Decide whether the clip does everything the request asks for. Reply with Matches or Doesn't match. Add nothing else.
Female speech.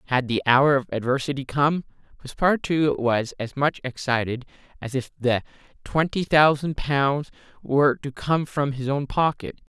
Doesn't match